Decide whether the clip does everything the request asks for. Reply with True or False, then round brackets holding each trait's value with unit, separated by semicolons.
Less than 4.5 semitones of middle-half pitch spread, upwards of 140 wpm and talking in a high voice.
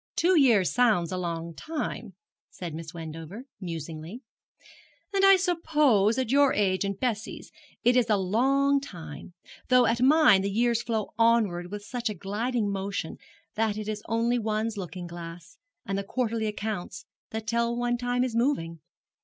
False (4.9 semitones; 160 wpm; 215 Hz)